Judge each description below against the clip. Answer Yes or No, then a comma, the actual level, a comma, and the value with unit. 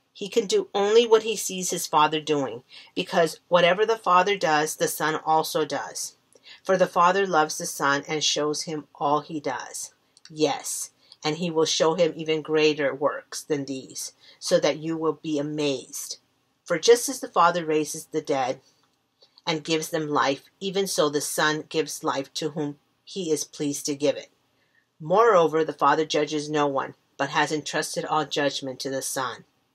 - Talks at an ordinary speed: Yes, average, 175 wpm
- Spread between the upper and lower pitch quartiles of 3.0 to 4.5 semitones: No, narrow, 2.6 semitones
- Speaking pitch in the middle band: Yes, medium, 155 Hz